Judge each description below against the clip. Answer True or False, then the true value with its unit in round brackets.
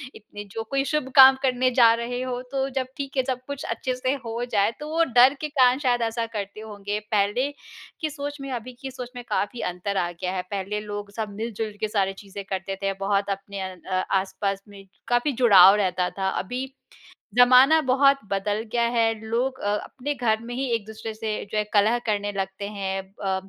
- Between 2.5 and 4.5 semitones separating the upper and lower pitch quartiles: True (4.1 semitones)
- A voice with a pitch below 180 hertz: False (220 Hz)